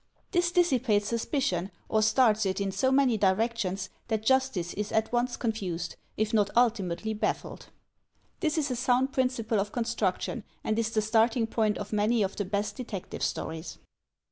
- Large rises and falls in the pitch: No, average, 3.2 semitones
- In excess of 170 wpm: No, average, 165 wpm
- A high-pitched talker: Yes, high, 220 Hz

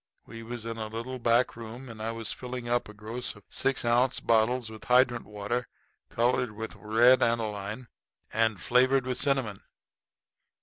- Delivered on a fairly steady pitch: Yes, narrow, 2.1 semitones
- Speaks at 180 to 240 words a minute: No, average, 165 wpm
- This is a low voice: Yes, low, 115 Hz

